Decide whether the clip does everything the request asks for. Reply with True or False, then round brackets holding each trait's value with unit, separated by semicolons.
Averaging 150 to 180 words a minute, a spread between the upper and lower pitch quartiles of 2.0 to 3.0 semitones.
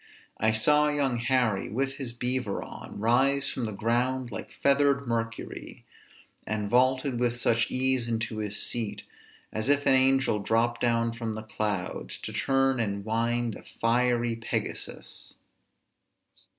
False (140 wpm; 2.7 semitones)